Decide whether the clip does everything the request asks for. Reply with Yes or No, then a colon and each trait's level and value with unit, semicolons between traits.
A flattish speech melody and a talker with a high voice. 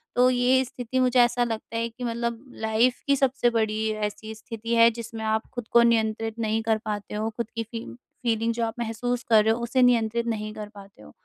Yes: narrow, 1.7 semitones; high, 230 Hz